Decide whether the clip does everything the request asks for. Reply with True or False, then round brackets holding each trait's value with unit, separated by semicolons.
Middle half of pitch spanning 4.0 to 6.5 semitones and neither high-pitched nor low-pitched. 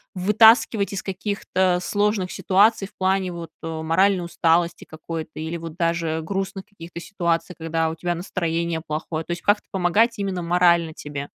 False (2.9 semitones; 175 Hz)